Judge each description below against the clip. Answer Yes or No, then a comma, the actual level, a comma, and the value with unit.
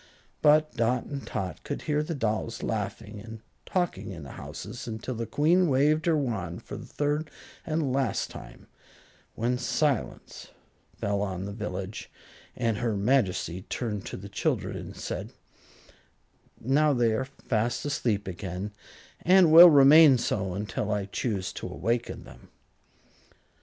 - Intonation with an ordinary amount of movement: No, wide, 6.2 semitones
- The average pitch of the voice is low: Yes, low, 115 Hz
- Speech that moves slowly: No, average, 145 wpm